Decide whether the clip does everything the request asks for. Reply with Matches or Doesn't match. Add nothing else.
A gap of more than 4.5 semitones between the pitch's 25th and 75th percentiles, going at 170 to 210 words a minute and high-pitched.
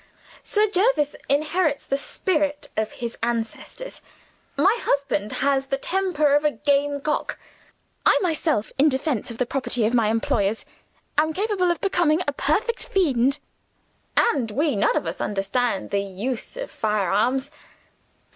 Doesn't match